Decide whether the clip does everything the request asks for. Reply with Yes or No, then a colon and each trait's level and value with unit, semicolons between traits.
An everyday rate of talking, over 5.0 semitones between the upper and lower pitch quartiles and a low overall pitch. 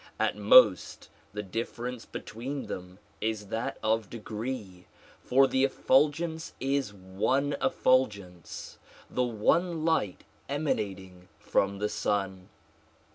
No: slow, 105 wpm; wide, 5.5 semitones; low, 115 Hz